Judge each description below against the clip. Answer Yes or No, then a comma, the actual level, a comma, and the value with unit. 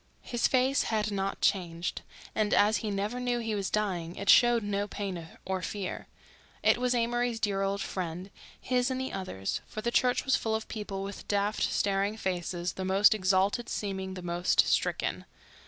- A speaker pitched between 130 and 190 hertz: No, high, 205 Hz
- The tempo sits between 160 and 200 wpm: Yes, average, 175 wpm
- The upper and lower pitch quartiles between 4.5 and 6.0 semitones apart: No, average, 3.1 semitones